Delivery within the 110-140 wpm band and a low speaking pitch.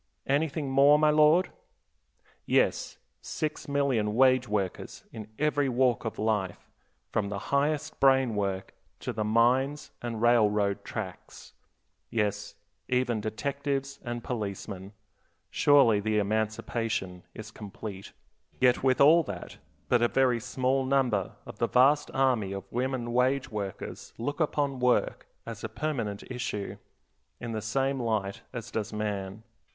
Yes: slow, 135 wpm; low, 120 Hz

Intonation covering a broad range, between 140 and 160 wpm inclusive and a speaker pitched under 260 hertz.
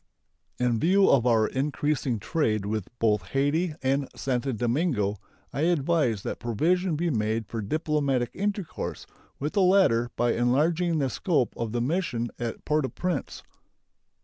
Yes: wide, 5.8 semitones; average, 145 wpm; low, 135 Hz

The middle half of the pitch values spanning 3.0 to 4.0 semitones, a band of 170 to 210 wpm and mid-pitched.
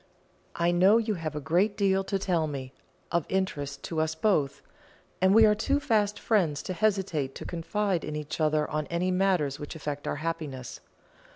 No: average, 4.5 semitones; average, 185 wpm; medium, 170 Hz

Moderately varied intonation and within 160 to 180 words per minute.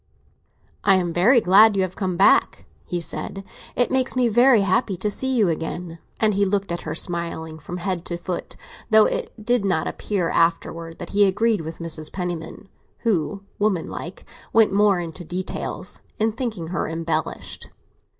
Yes: average, 3.9 semitones; average, 170 wpm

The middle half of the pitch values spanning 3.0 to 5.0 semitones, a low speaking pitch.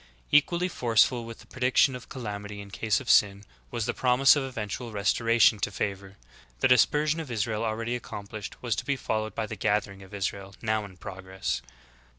Yes: average, 3.5 semitones; low, 110 Hz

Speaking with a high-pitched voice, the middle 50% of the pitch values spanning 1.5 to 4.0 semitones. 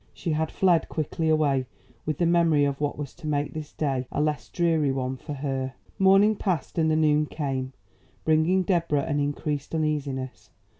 No: medium, 150 Hz; narrow, 2.5 semitones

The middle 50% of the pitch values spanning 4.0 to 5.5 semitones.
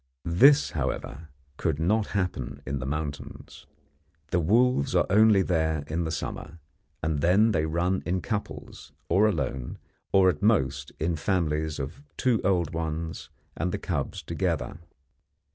Yes: average, 4.3 semitones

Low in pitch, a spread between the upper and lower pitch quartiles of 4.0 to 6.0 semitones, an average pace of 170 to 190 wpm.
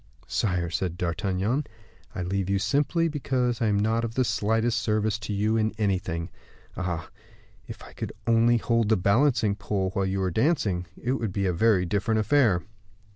No: low, 105 Hz; average, 3.5 semitones; average, 180 wpm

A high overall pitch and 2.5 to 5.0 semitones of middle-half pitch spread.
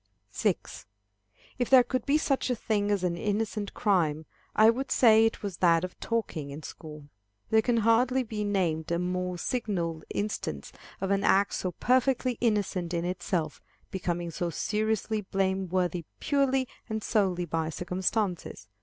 Yes: high, 195 Hz; average, 4.4 semitones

